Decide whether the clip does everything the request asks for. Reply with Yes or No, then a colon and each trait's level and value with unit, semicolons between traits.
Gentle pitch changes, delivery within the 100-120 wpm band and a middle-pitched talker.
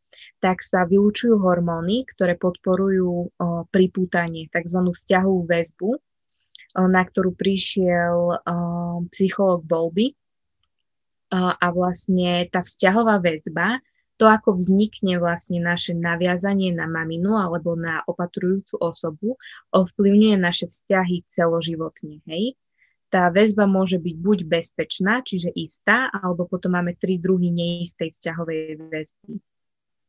Yes: narrow, 2.2 semitones; slow, 110 wpm; medium, 180 Hz